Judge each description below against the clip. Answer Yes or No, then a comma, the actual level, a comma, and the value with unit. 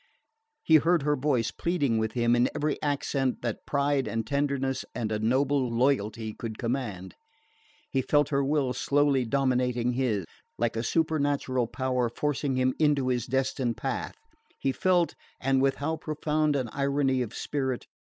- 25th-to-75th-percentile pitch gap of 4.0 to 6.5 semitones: No, average, 2.9 semitones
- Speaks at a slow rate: No, average, 155 wpm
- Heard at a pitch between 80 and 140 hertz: Yes, low, 135 Hz